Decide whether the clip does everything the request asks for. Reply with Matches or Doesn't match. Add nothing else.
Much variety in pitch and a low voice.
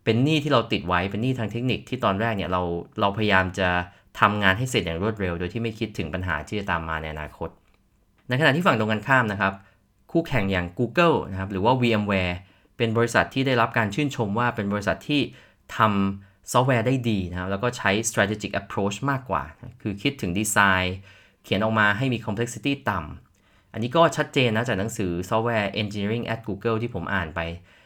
Doesn't match